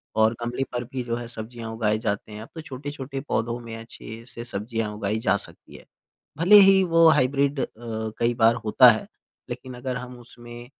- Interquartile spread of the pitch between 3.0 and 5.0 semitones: No, narrow, 2.6 semitones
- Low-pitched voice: Yes, low, 120 Hz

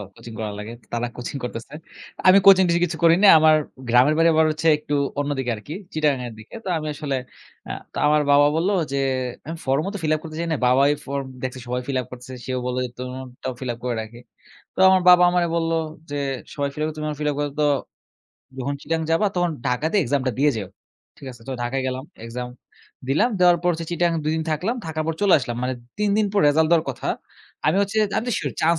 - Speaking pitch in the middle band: Yes, medium, 150 Hz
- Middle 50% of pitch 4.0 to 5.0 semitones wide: Yes, average, 4.4 semitones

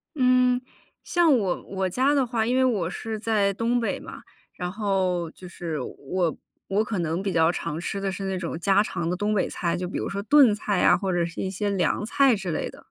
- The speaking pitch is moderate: No, high, 195 Hz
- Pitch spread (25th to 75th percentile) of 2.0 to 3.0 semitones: No, average, 4.2 semitones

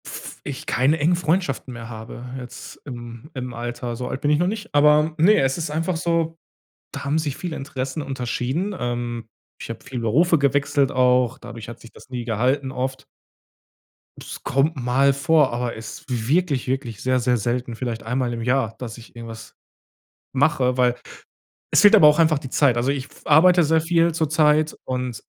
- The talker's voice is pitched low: Yes, low, 130 Hz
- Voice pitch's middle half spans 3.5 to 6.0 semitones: Yes, average, 4.2 semitones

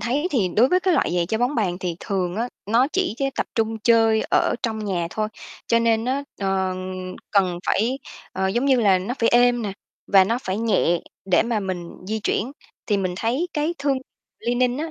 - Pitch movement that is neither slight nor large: Yes, average, 4.4 semitones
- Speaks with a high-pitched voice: Yes, high, 225 Hz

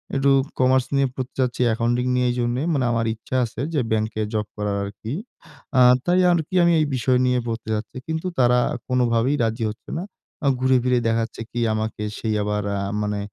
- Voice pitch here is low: Yes, low, 120 Hz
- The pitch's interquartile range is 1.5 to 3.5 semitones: Yes, average, 2.8 semitones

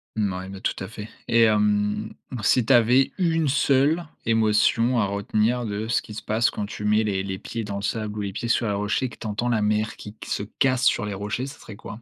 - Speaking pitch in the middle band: No, low, 110 Hz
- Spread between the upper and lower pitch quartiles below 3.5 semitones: Yes, narrow, 2.5 semitones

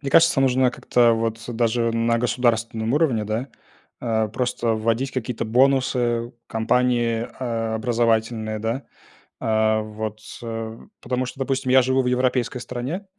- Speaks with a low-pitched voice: Yes, low, 120 Hz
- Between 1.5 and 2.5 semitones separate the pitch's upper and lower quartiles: Yes, narrow, 2.1 semitones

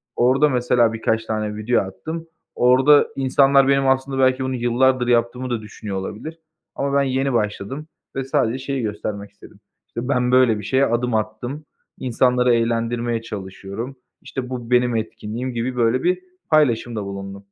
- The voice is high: No, low, 125 Hz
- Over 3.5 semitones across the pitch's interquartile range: No, average, 2.9 semitones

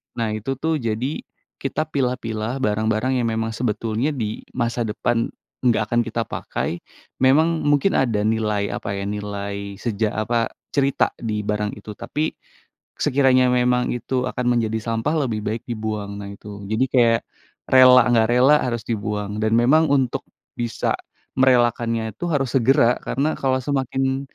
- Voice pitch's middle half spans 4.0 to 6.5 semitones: No, average, 3.3 semitones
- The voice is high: No, low, 120 Hz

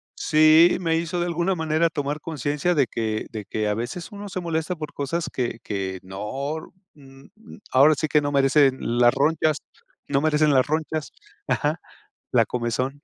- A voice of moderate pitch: Yes, medium, 150 Hz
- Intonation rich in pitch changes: No, average, 3.7 semitones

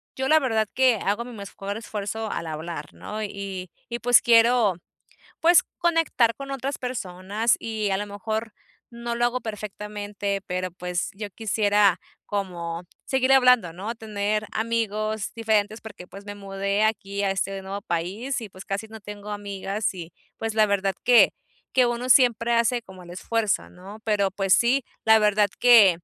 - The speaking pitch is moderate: No, high, 210 Hz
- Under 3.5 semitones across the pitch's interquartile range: Yes, average, 2.9 semitones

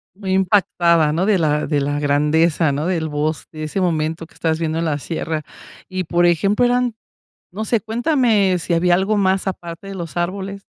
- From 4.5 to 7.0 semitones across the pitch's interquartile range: No, average, 3.7 semitones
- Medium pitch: Yes, medium, 175 Hz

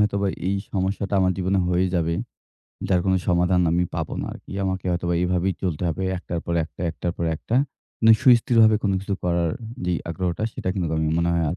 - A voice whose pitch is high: No, very low, 90 Hz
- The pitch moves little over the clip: Yes, narrow, 2.1 semitones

